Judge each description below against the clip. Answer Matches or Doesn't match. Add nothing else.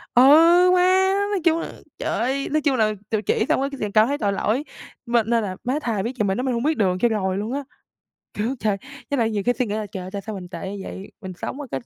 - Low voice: Doesn't match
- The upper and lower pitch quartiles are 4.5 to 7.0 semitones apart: Matches